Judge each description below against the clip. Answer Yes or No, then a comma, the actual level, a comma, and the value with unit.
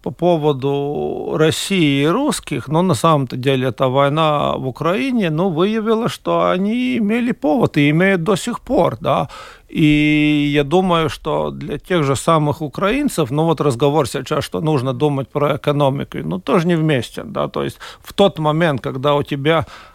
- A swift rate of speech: Yes, fast, 170 wpm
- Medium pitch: Yes, medium, 155 Hz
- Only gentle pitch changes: No, average, 3.6 semitones